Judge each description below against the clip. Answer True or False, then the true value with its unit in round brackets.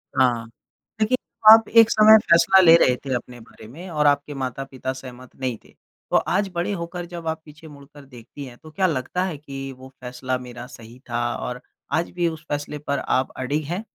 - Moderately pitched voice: True (145 Hz)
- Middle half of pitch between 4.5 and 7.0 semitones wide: True (5.0 semitones)